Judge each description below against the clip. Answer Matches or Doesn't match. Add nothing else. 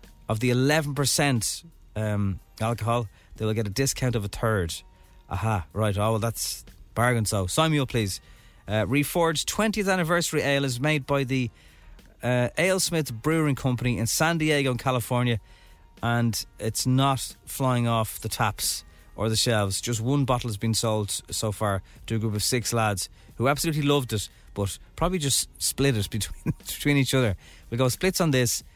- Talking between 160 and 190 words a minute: Matches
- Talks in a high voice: Doesn't match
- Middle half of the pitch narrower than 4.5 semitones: Doesn't match